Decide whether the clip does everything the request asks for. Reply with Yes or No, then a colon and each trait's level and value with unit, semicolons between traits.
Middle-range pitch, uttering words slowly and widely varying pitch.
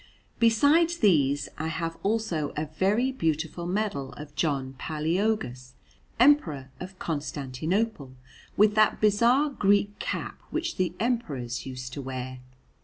Yes: medium, 165 Hz; slow, 120 wpm; wide, 7.6 semitones